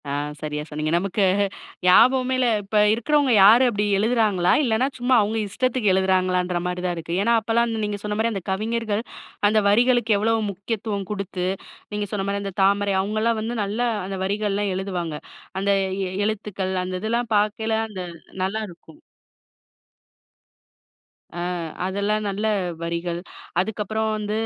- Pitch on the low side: No, high, 205 Hz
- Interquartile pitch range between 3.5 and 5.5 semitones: No, average, 2.8 semitones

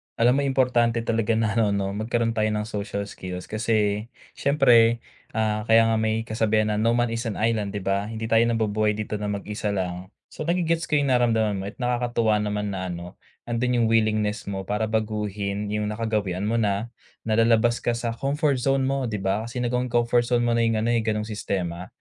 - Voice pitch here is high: No, low, 110 Hz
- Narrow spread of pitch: Yes, narrow, 2.2 semitones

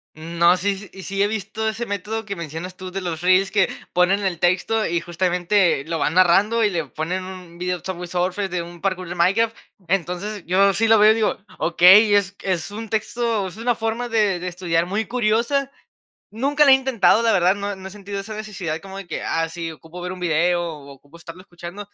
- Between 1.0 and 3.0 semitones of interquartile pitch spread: No, average, 3.5 semitones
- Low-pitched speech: No, high, 190 Hz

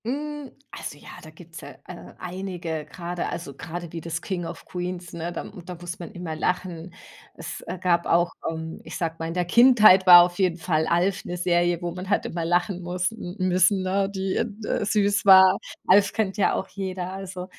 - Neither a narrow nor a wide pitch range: No, narrow, 1.9 semitones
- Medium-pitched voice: Yes, medium, 180 Hz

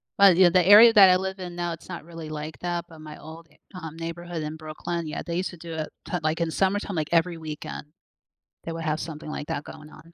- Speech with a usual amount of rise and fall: No, narrow, 2.2 semitones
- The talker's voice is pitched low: No, medium, 165 Hz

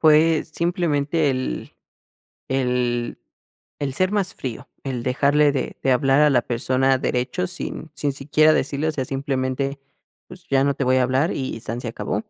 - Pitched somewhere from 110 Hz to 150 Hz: Yes, low, 135 Hz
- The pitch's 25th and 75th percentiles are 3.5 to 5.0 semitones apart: No, average, 2.8 semitones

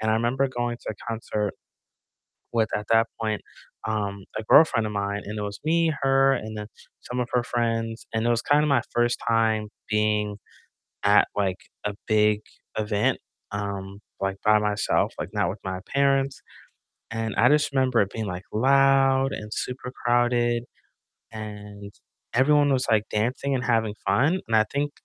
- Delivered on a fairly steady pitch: No, average, 3.6 semitones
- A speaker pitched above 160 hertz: No, low, 115 Hz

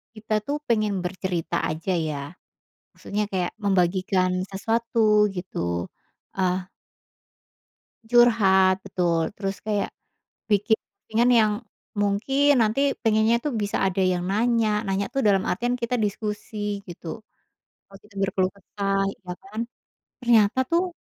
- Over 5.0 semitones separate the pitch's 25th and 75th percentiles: No, average, 3.1 semitones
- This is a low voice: No, high, 205 Hz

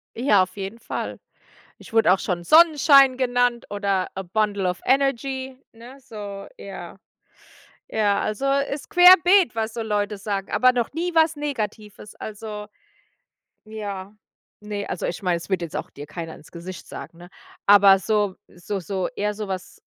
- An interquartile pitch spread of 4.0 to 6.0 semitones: Yes, average, 4.7 semitones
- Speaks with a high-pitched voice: Yes, high, 210 Hz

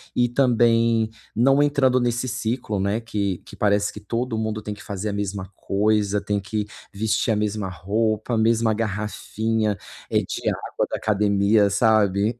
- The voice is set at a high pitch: No, low, 110 Hz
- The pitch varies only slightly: Yes, narrow, 2.1 semitones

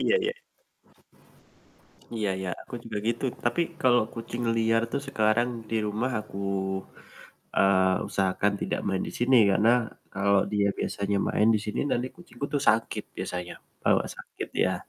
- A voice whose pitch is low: Yes, low, 110 Hz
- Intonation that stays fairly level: No, average, 3.3 semitones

